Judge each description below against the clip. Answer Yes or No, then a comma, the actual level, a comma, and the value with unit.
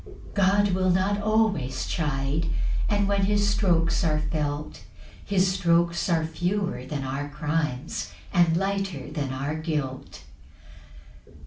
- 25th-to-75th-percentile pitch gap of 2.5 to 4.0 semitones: No, average, 4.7 semitones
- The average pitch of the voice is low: No, medium, 170 Hz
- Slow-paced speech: Yes, slow, 125 wpm